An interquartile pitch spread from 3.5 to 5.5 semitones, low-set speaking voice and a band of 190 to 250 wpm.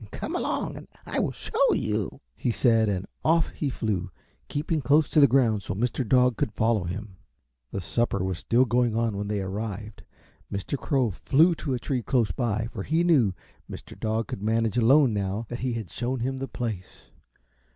Yes: average, 4.1 semitones; low, 115 Hz; average, 195 wpm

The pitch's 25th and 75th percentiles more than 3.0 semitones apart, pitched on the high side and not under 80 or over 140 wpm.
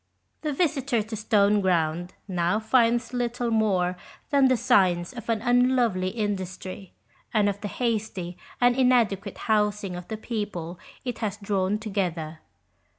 Yes: average, 4.2 semitones; high, 210 Hz; slow, 135 wpm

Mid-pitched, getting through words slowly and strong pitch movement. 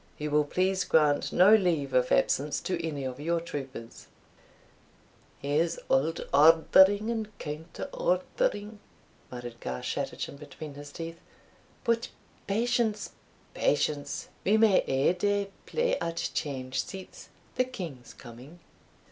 Yes: medium, 165 Hz; slow, 120 wpm; wide, 6.2 semitones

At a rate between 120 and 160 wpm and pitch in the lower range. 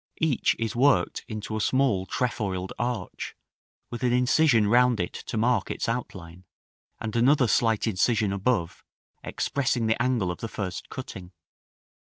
Yes: average, 145 wpm; low, 115 Hz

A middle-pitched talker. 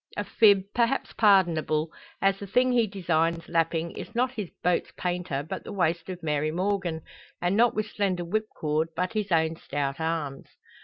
Yes: medium, 175 Hz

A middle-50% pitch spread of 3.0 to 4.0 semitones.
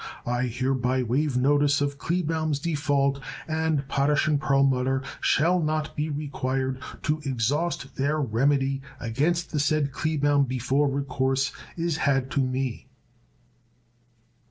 No: narrow, 2.5 semitones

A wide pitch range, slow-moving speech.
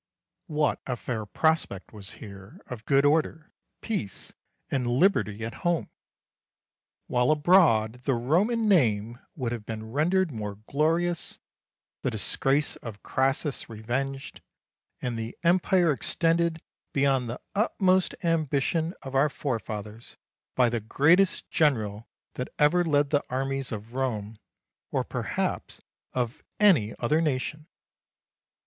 Yes: wide, 6.0 semitones; slow, 120 wpm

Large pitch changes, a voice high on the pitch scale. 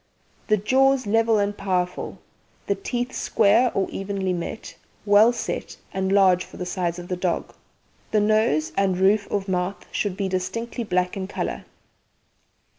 No: average, 2.9 semitones; high, 195 Hz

